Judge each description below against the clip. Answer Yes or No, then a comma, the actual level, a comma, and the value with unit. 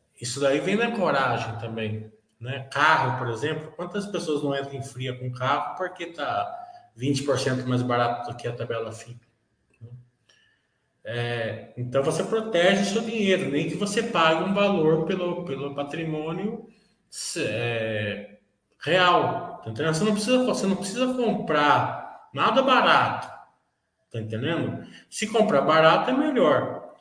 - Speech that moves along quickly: No, average, 140 wpm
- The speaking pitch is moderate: Yes, medium, 145 Hz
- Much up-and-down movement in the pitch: Yes, wide, 7.8 semitones